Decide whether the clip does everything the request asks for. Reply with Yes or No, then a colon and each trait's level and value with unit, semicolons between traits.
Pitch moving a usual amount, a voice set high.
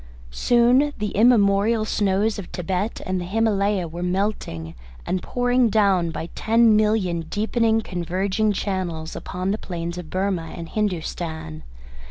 Yes: average, 3.7 semitones; high, 195 Hz